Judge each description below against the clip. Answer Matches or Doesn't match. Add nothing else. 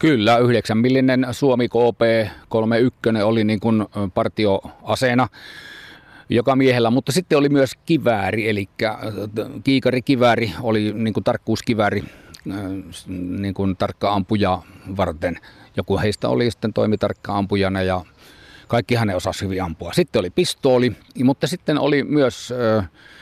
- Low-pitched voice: Matches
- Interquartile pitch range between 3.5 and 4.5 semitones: Matches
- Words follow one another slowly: Doesn't match